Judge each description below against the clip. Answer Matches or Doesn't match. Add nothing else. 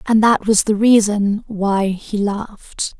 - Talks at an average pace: Matches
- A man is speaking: Doesn't match